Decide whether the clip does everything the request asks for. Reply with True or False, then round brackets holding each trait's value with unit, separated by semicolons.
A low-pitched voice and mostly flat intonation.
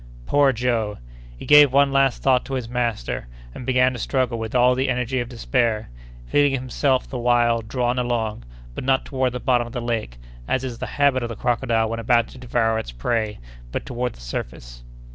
True (120 Hz; 2.2 semitones)